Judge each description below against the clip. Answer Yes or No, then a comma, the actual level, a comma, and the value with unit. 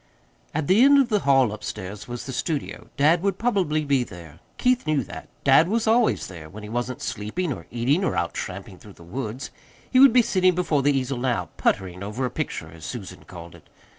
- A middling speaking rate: No, fast, 215 wpm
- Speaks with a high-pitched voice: No, low, 135 Hz